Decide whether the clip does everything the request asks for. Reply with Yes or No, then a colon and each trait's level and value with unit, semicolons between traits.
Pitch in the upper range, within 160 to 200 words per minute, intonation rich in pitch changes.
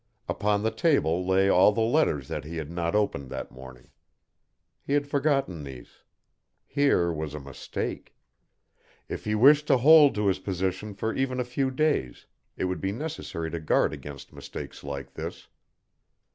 No: low, 100 Hz; average, 165 wpm; wide, 8.8 semitones